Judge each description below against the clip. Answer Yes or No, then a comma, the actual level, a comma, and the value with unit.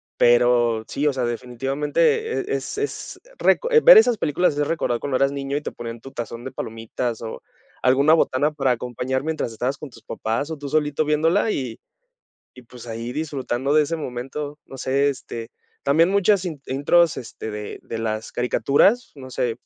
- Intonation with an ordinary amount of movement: Yes, average, 4.2 semitones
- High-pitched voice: No, low, 135 Hz